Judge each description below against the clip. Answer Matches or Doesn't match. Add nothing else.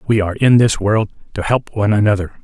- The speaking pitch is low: Matches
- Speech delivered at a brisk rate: Matches